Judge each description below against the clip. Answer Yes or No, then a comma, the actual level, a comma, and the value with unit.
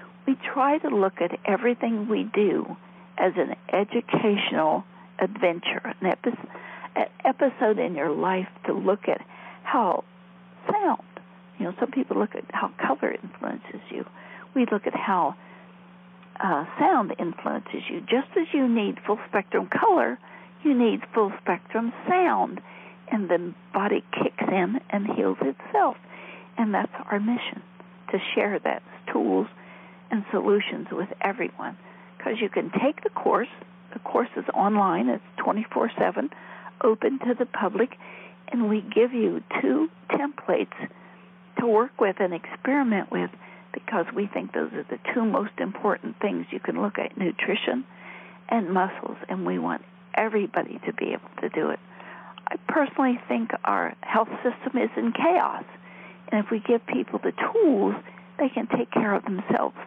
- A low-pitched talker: No, high, 215 Hz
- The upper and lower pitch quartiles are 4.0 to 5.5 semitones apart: Yes, average, 4.9 semitones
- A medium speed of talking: Yes, average, 150 wpm